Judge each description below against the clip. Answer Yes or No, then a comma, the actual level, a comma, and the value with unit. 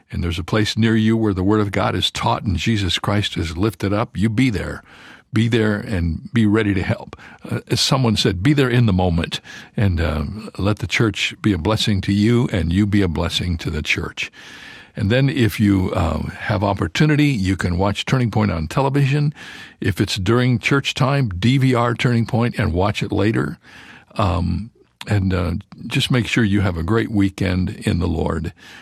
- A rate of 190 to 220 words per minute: Yes, average, 200 wpm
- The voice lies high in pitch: No, low, 105 Hz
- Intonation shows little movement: No, average, 3.6 semitones